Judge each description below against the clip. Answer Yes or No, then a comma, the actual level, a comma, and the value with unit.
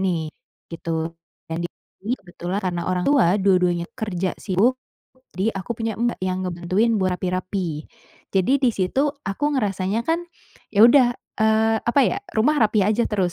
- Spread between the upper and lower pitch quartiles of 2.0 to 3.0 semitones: No, average, 3.6 semitones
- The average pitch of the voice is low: No, high, 195 Hz